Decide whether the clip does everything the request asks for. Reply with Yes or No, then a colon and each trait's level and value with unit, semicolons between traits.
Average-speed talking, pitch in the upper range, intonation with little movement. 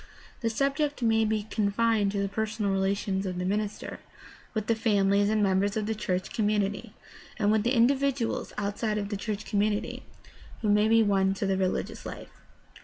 Yes: average, 185 wpm; high, 210 Hz; narrow, 1.9 semitones